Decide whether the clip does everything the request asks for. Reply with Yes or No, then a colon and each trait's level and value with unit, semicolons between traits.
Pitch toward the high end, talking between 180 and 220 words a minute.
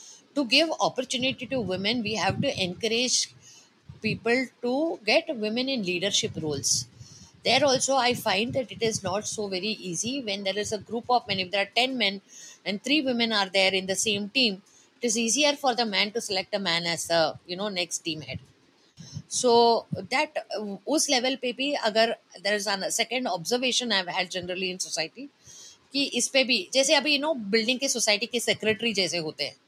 Yes: high, 220 Hz; fast, 190 wpm